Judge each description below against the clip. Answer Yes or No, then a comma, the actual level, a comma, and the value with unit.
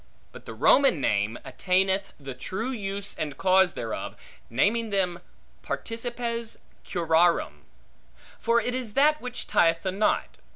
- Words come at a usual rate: No, slow, 130 wpm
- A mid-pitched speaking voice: No, high, 195 Hz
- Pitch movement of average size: No, wide, 5.8 semitones